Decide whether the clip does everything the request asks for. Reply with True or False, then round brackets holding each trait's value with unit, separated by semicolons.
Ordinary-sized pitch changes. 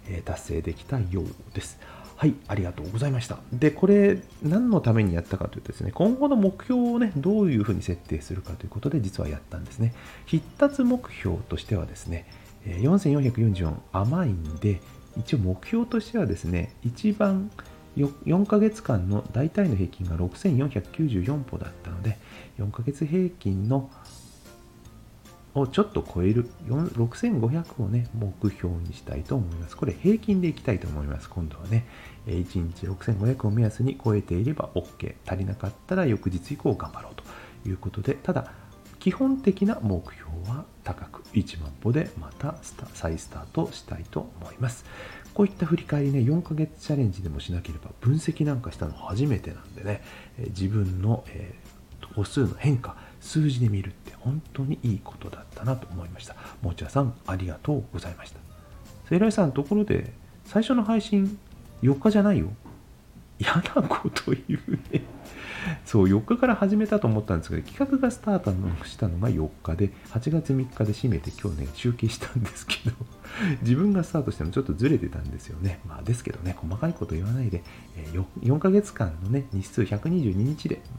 False (7.7 semitones)